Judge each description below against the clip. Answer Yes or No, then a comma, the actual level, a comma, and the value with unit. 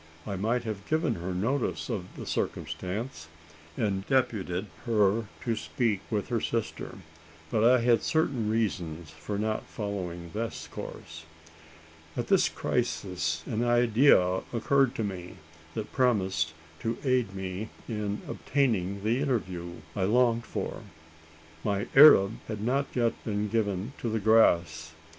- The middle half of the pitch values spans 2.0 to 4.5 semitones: Yes, average, 4.1 semitones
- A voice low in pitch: Yes, low, 105 Hz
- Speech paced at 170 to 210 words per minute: No, slow, 135 wpm